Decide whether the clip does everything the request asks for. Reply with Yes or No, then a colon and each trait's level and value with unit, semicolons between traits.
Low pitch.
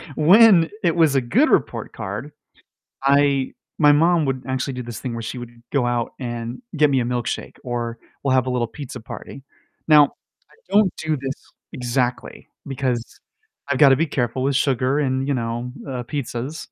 Yes: low, 130 Hz